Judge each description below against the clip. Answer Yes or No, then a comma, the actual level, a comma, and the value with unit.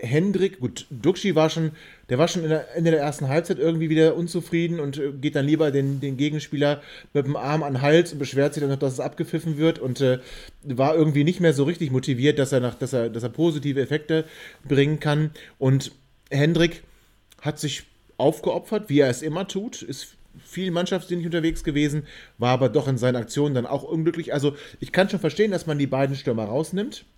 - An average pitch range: Yes, average, 3.0 semitones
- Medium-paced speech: No, fast, 205 wpm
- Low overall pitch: No, medium, 150 Hz